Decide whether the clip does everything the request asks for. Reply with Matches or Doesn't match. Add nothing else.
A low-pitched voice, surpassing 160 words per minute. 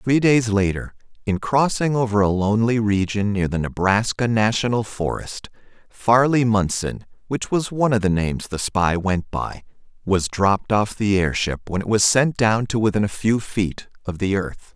Matches